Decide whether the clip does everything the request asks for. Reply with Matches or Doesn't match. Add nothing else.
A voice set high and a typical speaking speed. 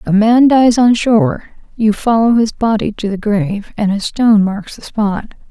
Matches